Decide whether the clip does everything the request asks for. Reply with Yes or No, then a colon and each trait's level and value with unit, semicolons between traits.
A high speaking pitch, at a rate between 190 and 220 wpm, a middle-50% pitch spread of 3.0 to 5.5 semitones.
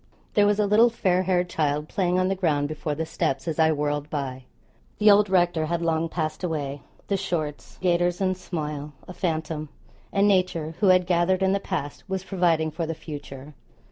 No: medium, 170 Hz; average, 195 wpm; average, 3.5 semitones